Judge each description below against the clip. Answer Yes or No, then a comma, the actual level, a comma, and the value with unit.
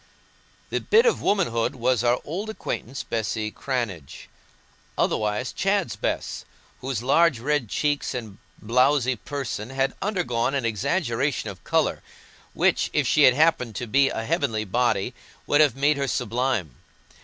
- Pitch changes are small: No, average, 4.2 semitones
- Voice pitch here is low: Yes, low, 125 Hz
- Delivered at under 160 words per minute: Yes, average, 145 wpm